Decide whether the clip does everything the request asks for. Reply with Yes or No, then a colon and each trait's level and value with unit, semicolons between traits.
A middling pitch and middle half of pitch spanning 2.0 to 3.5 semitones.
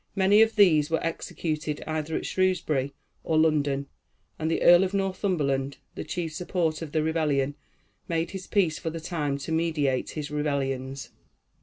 Yes: medium, 160 Hz; average, 3.2 semitones